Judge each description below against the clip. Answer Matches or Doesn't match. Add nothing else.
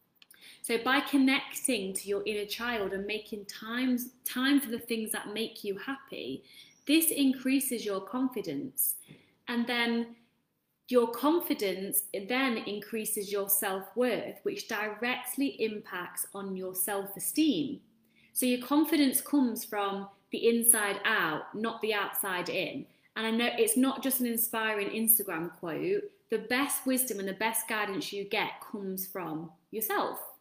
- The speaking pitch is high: Matches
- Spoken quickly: Doesn't match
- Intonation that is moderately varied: Matches